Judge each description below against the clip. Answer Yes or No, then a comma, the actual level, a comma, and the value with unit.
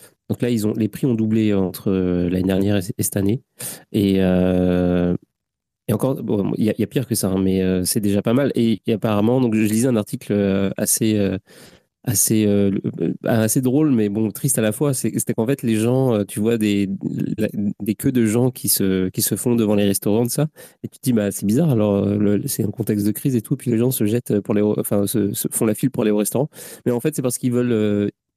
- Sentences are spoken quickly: Yes, fast, 240 wpm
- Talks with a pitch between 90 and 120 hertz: Yes, low, 110 Hz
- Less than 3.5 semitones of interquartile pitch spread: Yes, average, 3.1 semitones